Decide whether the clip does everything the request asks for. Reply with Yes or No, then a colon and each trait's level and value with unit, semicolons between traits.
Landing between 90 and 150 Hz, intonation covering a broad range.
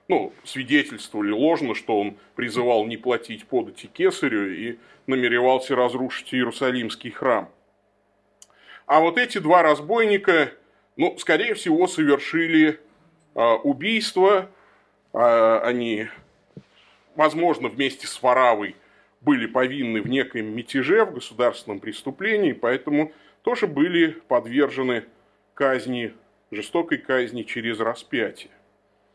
Yes: low, 135 Hz; wide, 8.3 semitones